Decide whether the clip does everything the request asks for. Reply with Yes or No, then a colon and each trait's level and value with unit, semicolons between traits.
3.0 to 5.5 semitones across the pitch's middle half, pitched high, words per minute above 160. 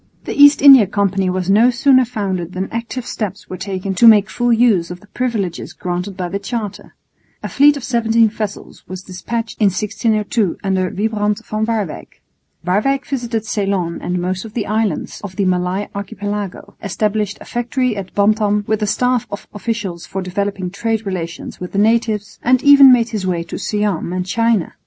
Yes: average, 3.4 semitones; high, 205 Hz; average, 180 wpm